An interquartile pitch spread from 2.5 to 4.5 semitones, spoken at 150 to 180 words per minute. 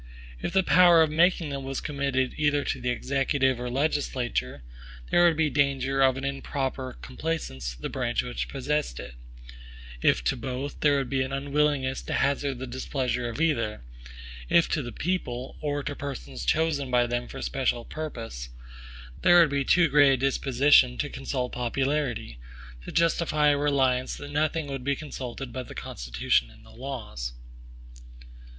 Yes: average, 2.9 semitones; average, 170 wpm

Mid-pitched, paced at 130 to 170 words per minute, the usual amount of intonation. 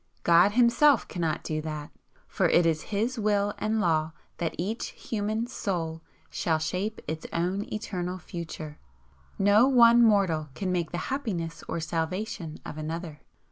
Yes: medium, 180 Hz; average, 145 wpm; average, 4.9 semitones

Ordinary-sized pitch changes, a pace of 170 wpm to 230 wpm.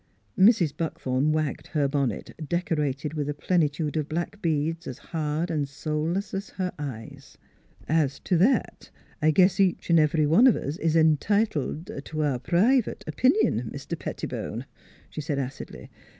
Yes: average, 3.3 semitones; average, 175 wpm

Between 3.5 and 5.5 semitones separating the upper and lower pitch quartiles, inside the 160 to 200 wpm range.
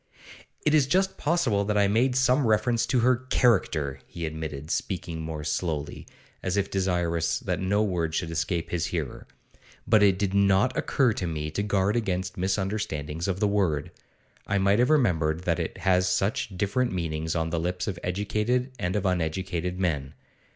Yes: average, 4.1 semitones; average, 180 wpm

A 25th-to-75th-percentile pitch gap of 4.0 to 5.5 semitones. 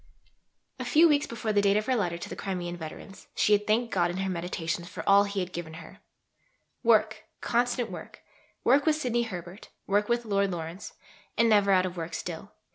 Yes: average, 4.7 semitones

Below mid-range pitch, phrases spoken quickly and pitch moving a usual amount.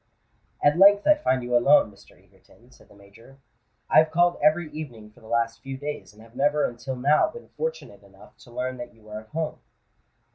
Yes: low, 130 Hz; fast, 210 wpm; average, 5.0 semitones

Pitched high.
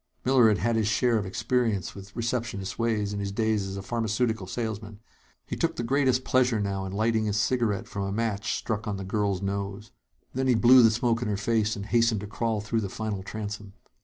No: low, 110 Hz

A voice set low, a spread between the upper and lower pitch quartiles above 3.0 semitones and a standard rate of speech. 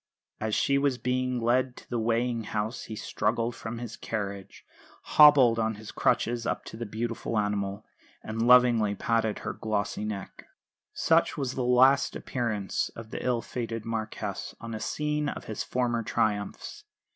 No: low, 115 Hz; narrow, 2.4 semitones; average, 160 wpm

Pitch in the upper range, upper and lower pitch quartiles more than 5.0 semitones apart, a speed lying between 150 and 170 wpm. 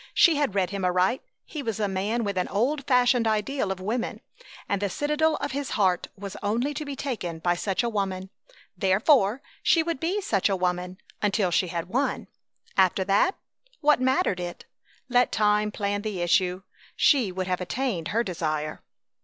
No: high, 205 Hz; wide, 5.6 semitones; average, 180 wpm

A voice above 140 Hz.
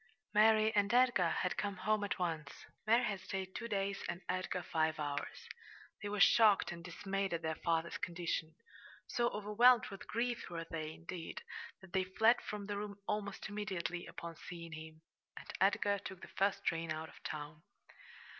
Yes: high, 190 Hz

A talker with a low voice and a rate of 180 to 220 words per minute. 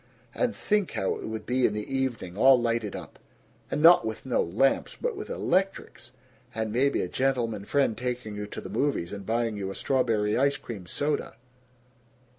Yes: low, 120 Hz; average, 185 wpm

